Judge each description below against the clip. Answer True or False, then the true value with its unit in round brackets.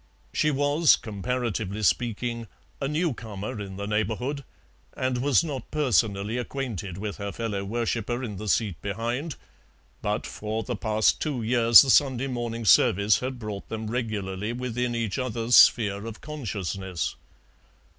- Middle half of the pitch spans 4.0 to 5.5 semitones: False (3.5 semitones)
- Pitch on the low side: True (115 Hz)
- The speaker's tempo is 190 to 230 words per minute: False (145 wpm)